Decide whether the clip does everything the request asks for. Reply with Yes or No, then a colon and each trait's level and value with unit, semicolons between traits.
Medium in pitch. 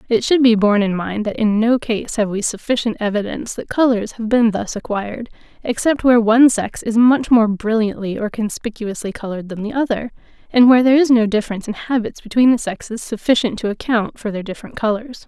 No: high, 225 Hz